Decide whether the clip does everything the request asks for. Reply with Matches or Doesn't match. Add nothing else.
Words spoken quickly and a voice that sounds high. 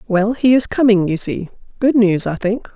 Matches